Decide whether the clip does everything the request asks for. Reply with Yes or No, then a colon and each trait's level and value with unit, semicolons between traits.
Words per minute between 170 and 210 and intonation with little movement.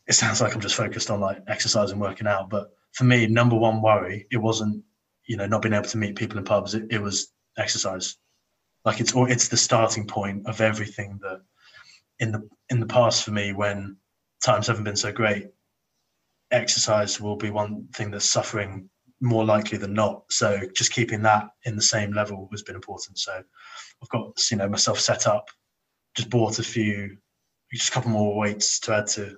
Yes: average, 200 wpm; narrow, 1.8 semitones